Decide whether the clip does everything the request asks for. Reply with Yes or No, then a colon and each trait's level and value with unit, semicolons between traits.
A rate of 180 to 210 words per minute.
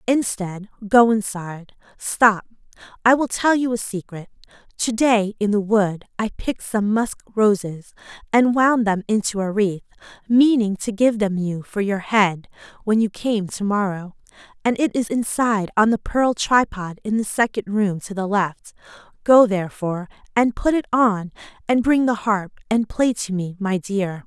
No: average, 170 wpm